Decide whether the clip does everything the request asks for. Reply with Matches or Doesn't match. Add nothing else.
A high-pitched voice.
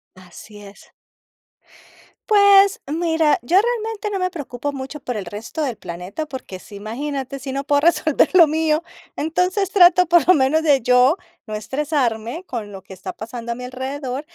Matches